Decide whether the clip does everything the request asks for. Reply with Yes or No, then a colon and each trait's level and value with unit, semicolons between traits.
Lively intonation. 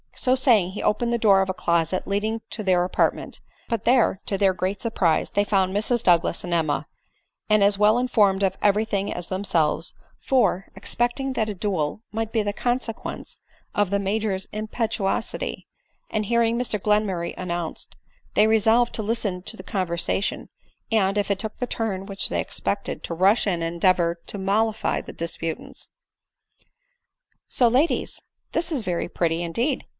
No: average, 3.4 semitones